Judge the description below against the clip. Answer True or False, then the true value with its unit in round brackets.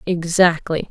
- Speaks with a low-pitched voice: False (170 Hz)